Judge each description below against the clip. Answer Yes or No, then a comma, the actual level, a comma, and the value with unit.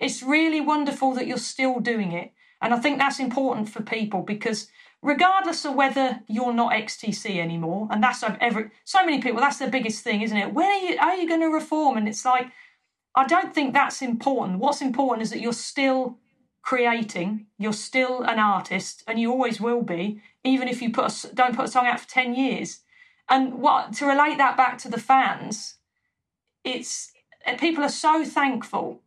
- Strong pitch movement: No, average, 3.6 semitones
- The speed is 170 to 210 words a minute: Yes, average, 195 wpm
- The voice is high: Yes, very high, 255 Hz